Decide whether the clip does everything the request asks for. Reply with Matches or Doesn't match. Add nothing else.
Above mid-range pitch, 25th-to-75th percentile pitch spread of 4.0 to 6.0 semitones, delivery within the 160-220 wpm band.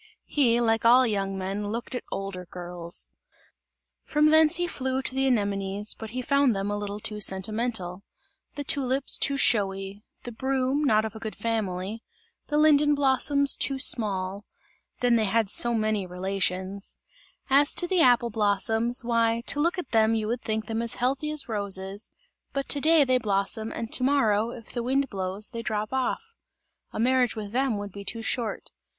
Matches